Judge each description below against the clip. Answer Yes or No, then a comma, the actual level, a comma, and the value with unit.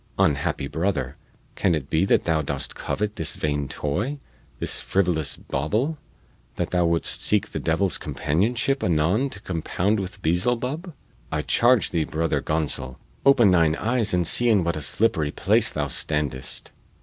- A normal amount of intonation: No, wide, 6.0 semitones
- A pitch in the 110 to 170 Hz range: No, very low, 85 Hz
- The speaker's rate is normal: Yes, average, 155 wpm